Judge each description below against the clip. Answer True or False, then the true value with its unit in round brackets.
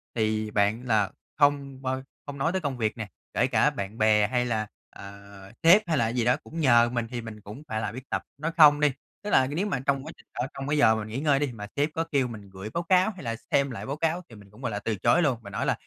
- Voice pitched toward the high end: False (125 Hz)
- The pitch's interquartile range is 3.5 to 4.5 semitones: False (5.0 semitones)